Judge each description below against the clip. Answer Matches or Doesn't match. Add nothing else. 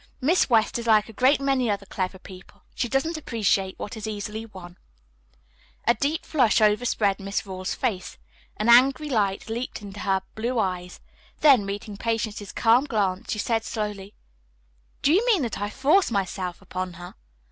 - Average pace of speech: Matches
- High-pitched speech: Matches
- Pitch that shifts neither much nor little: Matches